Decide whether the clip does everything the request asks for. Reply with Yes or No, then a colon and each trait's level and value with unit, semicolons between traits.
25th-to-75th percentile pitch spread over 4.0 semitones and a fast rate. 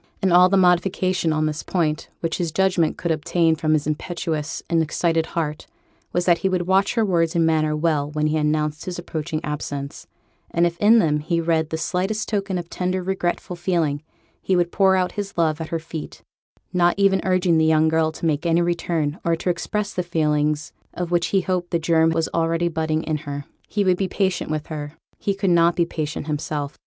No: narrow, 2.5 semitones; fast, 210 wpm